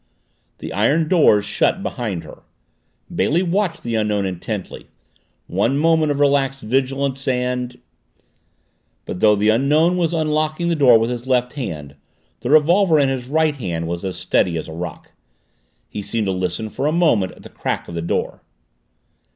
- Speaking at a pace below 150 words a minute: No, average, 165 wpm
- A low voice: Yes, low, 125 Hz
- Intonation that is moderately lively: No, wide, 7.0 semitones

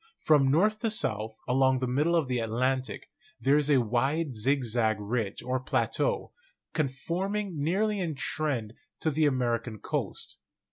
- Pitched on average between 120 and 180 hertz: Yes, low, 135 Hz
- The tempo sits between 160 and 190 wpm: No, average, 150 wpm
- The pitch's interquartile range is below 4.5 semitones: No, average, 4.8 semitones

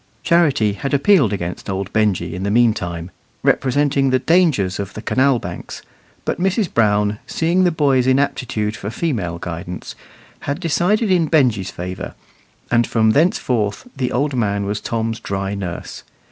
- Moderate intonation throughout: No, wide, 6.4 semitones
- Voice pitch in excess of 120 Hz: No, low, 115 Hz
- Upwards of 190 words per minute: No, average, 150 wpm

